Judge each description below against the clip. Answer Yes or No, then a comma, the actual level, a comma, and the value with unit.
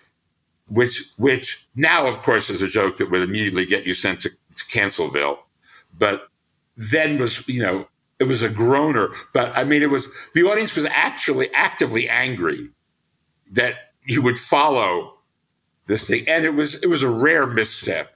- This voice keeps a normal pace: Yes, average, 170 wpm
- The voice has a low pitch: Yes, low, 120 Hz